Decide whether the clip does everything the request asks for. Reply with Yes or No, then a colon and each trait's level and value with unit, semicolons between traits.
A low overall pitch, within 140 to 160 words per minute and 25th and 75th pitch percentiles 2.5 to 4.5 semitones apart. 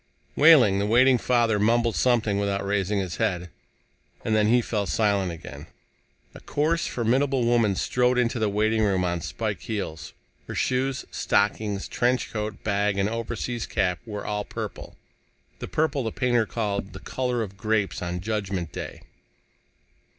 Yes: low, 110 Hz; average, 155 wpm; average, 3.3 semitones